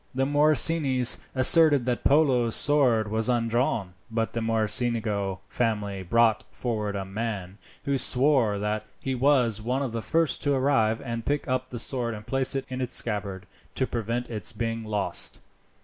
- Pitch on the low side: Yes, low, 115 Hz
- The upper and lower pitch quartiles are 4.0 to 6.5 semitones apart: No, average, 3.5 semitones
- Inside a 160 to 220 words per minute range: Yes, average, 165 wpm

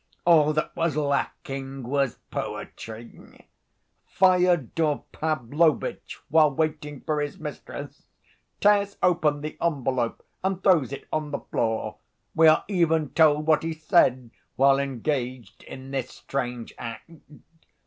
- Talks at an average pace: No, slow, 120 wpm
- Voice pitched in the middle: Yes, medium, 150 Hz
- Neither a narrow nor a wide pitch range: Yes, average, 3.3 semitones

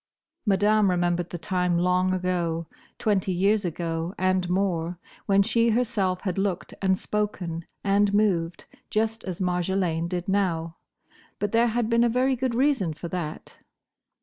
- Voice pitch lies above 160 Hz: Yes, medium, 185 Hz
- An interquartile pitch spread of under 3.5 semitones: Yes, average, 3.1 semitones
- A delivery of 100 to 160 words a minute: Yes, average, 140 wpm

